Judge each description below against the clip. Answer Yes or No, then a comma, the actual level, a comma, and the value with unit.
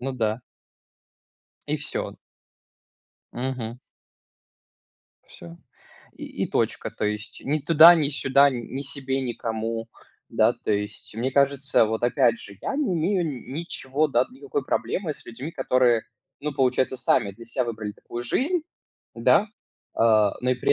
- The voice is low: Yes, low, 130 Hz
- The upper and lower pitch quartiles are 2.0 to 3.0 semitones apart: No, average, 3.8 semitones